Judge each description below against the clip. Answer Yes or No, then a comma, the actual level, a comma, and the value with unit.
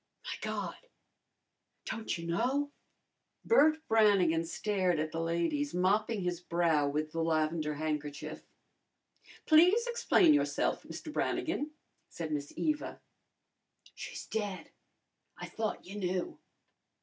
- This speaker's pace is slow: Yes, slow, 115 wpm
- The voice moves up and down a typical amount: No, wide, 7.0 semitones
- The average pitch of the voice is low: No, medium, 180 Hz